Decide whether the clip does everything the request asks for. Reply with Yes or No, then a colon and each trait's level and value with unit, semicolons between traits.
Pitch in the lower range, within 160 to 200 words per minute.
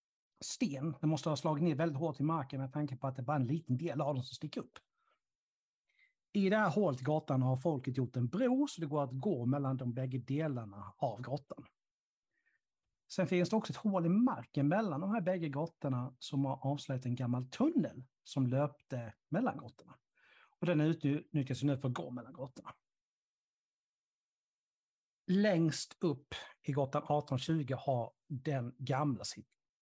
No: medium, 145 Hz; average, 175 wpm